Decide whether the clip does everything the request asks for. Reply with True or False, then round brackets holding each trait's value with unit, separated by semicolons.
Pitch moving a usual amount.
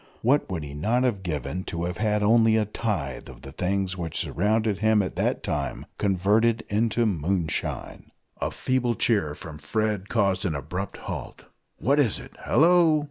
True (4.1 semitones)